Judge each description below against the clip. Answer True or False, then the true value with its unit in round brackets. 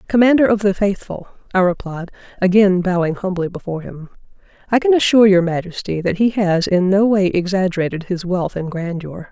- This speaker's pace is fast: False (175 wpm)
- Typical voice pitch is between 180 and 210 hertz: True (190 Hz)